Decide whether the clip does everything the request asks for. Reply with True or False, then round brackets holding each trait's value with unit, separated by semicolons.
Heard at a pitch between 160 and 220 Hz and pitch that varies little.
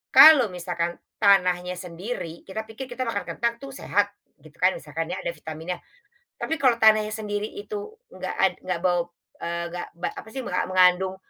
False (190 Hz; 4.1 semitones)